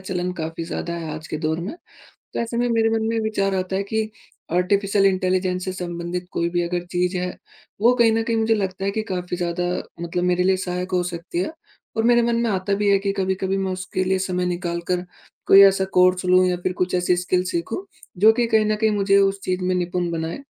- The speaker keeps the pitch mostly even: Yes, narrow, 2.1 semitones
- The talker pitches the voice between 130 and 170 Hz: No, medium, 185 Hz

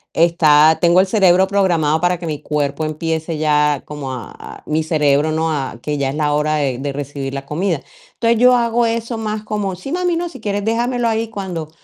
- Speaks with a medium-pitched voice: Yes, medium, 165 Hz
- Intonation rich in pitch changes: Yes, wide, 6.2 semitones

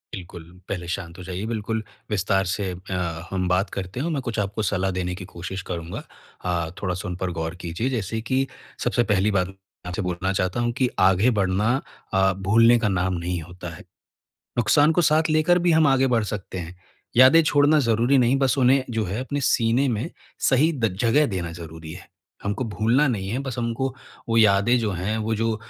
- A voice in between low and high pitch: No, low, 105 Hz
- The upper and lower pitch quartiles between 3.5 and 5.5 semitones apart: Yes, average, 5.0 semitones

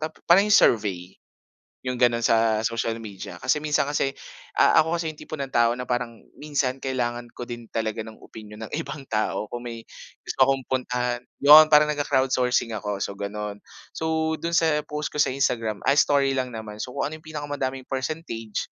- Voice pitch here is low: Yes, low, 125 Hz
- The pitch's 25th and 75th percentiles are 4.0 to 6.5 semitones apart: Yes, average, 4.5 semitones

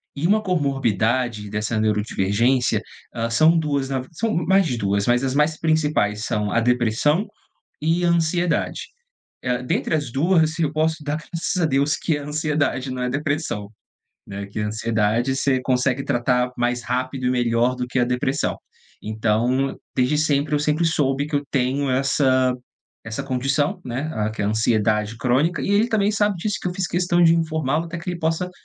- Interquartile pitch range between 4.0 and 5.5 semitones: Yes, average, 4.7 semitones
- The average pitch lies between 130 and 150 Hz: Yes, low, 135 Hz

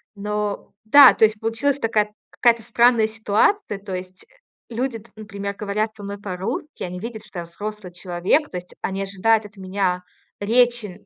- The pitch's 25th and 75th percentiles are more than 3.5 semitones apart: No, average, 2.7 semitones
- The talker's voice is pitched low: No, high, 210 Hz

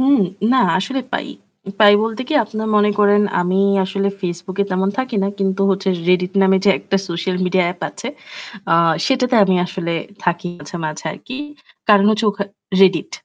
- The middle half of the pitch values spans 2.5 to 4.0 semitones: Yes, average, 2.9 semitones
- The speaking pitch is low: No, high, 195 Hz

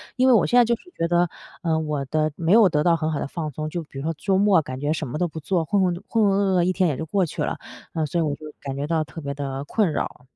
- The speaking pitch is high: No, medium, 160 Hz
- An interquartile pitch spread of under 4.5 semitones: Yes, average, 3.7 semitones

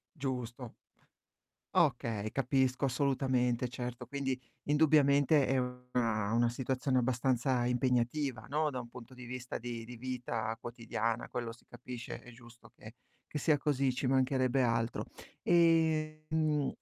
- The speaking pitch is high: No, low, 125 Hz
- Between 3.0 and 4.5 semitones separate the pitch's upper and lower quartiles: No, narrow, 2.4 semitones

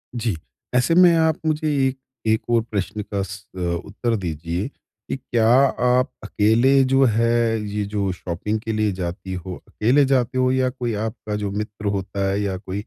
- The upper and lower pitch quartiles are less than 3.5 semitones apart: No, average, 4.2 semitones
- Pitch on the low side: Yes, low, 110 Hz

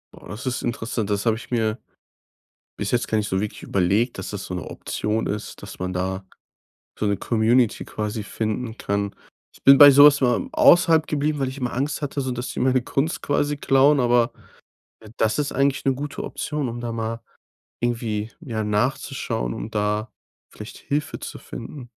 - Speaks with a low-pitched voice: Yes, low, 120 Hz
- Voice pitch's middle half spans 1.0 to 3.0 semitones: No, average, 4.4 semitones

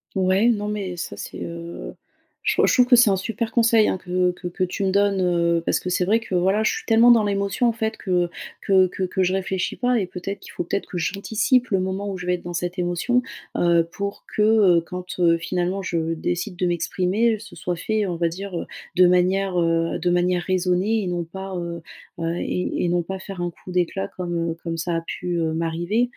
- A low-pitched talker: No, medium, 185 Hz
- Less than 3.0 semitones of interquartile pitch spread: Yes, narrow, 2.4 semitones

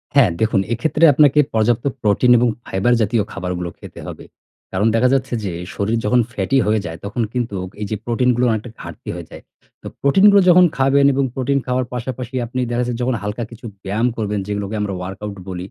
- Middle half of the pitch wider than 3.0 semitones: Yes, average, 3.8 semitones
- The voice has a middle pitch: No, low, 115 Hz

